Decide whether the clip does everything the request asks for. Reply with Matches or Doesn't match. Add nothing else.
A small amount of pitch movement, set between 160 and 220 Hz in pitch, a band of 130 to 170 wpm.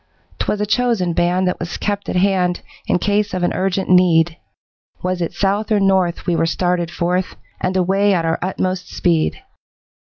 Doesn't match